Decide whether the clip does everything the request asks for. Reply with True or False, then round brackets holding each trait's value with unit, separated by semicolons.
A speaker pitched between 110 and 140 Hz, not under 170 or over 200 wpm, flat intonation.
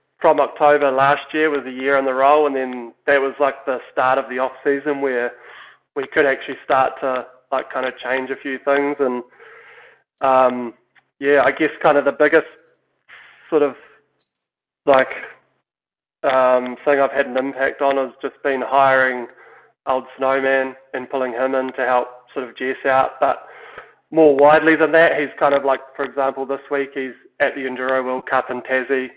True (135 Hz; 185 wpm; 1.3 semitones)